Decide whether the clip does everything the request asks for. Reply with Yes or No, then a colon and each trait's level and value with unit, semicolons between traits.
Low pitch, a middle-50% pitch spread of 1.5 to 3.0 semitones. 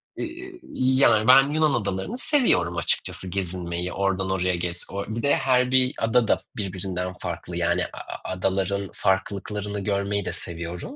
No: low, 100 Hz; wide, 5.4 semitones